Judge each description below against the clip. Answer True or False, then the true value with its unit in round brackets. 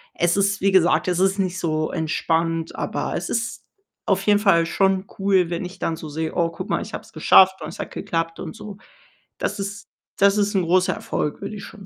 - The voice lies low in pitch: False (185 Hz)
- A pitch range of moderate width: True (3.0 semitones)